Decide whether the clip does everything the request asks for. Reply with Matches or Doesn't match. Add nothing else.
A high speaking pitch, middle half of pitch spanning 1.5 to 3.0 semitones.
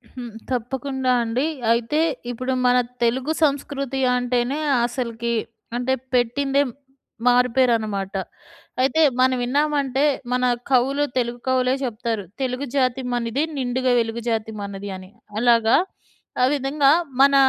Matches